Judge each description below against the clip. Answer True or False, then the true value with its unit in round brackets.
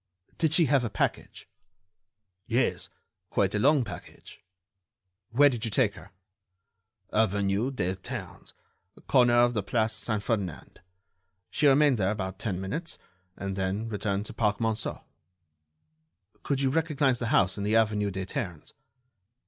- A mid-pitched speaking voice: False (110 Hz)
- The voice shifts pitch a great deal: False (4.2 semitones)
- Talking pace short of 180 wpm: True (145 wpm)